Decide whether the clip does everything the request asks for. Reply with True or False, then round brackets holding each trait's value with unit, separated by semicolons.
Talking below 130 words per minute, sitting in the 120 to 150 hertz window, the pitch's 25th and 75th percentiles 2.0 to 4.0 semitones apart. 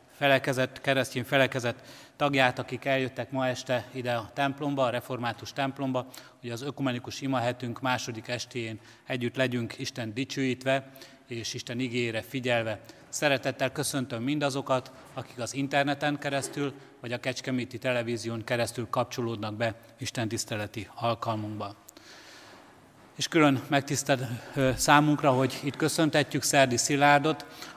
True (115 wpm; 130 Hz; 2.4 semitones)